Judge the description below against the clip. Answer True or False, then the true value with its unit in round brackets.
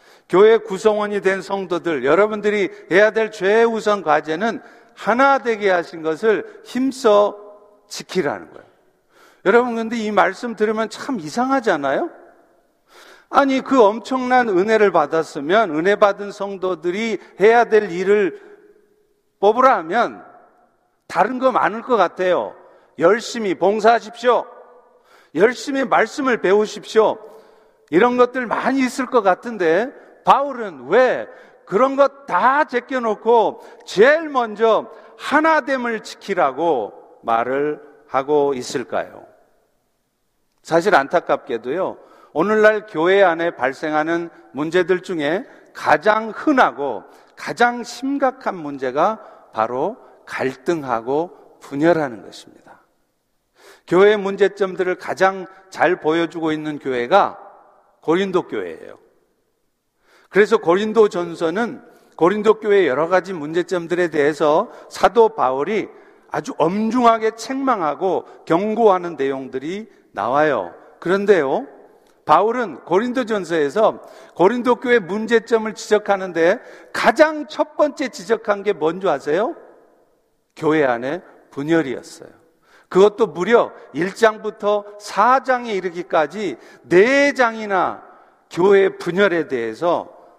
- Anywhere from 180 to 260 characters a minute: True (250 characters per minute)